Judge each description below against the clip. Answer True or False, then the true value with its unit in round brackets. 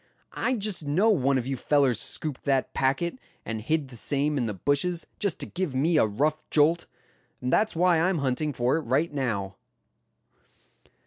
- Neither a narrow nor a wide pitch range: True (4.4 semitones)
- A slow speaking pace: False (180 wpm)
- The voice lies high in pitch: False (145 Hz)